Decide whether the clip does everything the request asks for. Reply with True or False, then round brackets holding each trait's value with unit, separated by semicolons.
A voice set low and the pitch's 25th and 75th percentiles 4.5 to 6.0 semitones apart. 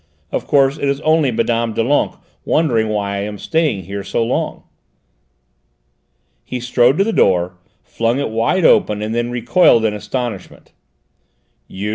True (115 Hz; 4.8 semitones)